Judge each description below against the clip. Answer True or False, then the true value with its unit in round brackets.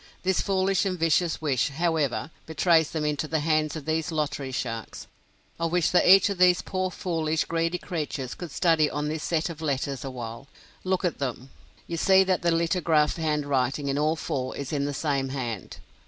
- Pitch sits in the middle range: True (155 Hz)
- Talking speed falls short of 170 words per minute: False (185 wpm)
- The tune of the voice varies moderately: True (3.4 semitones)